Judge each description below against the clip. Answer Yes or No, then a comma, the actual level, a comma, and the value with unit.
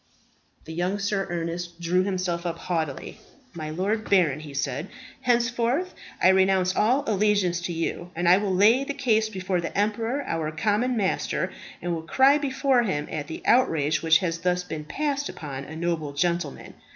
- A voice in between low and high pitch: Yes, medium, 180 Hz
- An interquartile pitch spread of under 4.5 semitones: No, average, 4.8 semitones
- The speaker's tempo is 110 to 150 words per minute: No, average, 175 wpm